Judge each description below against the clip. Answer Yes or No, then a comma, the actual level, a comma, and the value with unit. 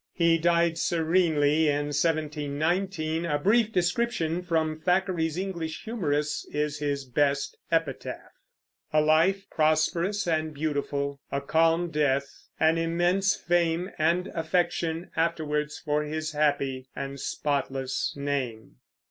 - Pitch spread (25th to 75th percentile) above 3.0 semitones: No, narrow, 2.6 semitones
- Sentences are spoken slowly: Yes, slow, 115 wpm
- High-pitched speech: No, medium, 160 Hz